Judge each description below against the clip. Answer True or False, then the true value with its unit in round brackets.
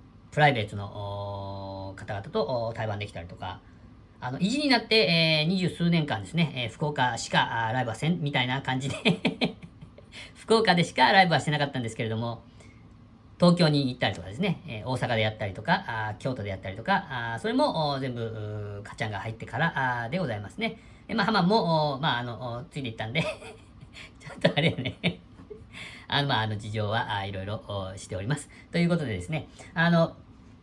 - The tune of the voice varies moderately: False (6.4 semitones)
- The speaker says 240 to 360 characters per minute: False (375 characters per minute)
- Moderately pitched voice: False (120 Hz)